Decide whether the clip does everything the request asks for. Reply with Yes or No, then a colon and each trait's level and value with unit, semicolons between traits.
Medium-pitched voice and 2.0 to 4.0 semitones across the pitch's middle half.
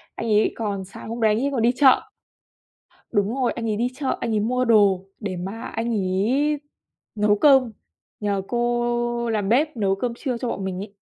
No: high, 230 Hz; average, 3.1 semitones